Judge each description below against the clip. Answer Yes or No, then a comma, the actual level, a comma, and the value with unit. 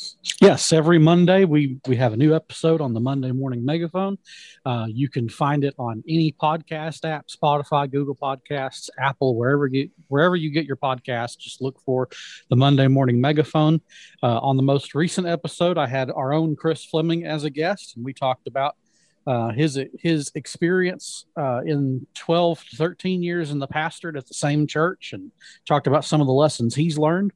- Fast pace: No, average, 185 wpm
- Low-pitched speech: No, medium, 150 Hz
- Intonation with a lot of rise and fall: No, average, 3.5 semitones